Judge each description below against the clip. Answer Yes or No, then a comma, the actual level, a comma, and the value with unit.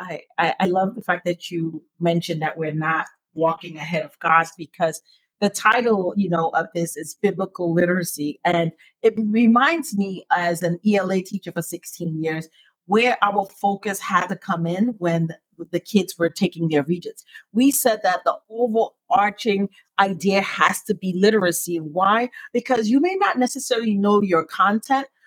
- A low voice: No, medium, 185 Hz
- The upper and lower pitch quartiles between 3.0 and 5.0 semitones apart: Yes, average, 4.0 semitones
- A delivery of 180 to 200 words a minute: No, average, 165 wpm